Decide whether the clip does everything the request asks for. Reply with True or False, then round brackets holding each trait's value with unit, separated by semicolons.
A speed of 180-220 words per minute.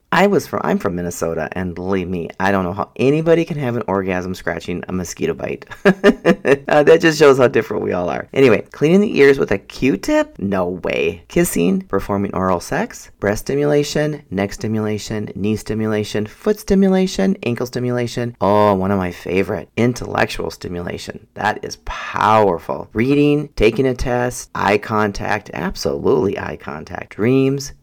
False (155 wpm)